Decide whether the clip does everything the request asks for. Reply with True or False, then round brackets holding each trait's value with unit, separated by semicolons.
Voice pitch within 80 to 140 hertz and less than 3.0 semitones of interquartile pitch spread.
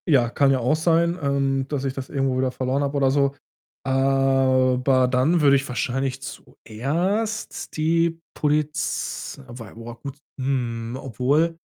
True (135 Hz; 2.4 semitones)